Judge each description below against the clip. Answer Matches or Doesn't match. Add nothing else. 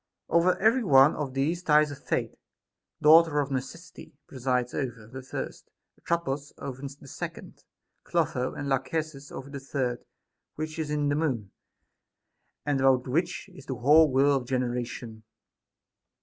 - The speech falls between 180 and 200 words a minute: Doesn't match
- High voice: Doesn't match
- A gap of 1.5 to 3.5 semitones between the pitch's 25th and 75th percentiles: Matches